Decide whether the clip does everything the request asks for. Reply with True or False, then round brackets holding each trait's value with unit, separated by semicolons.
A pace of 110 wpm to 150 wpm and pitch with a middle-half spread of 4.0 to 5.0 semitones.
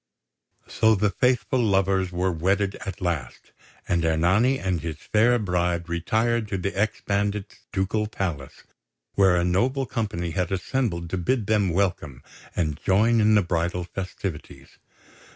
False (145 wpm; 3.5 semitones)